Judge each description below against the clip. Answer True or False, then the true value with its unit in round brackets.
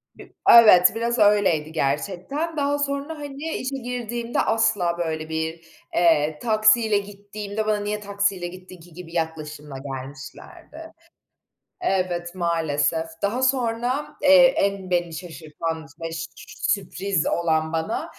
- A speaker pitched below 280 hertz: True (190 Hz)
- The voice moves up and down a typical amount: False (6.0 semitones)